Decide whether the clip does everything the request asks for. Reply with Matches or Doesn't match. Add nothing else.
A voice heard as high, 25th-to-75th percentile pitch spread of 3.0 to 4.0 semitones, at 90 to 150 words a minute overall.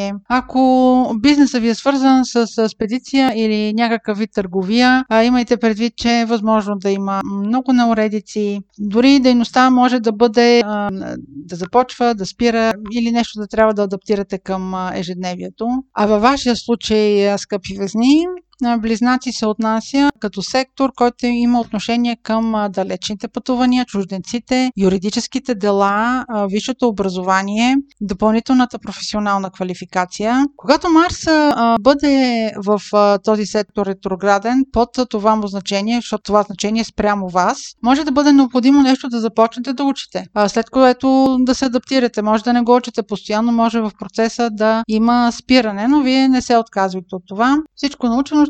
Matches